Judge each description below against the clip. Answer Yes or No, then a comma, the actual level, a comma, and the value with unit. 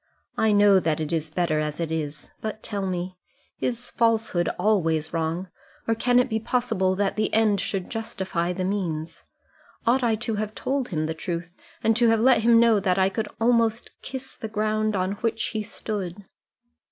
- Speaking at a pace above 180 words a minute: Yes, average, 190 wpm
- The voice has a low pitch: No, high, 205 Hz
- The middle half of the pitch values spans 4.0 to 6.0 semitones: Yes, average, 4.3 semitones